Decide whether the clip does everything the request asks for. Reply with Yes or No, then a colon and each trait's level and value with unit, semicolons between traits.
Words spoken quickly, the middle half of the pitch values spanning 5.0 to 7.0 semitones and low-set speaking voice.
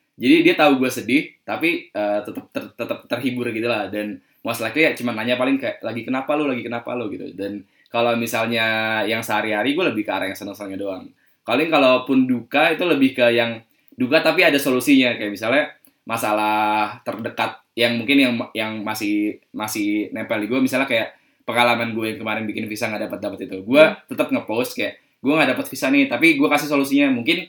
Yes: fast, 195 wpm; wide, 5.4 semitones; low, 120 Hz